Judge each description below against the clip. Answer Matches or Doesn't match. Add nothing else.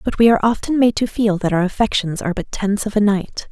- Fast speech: Matches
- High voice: Matches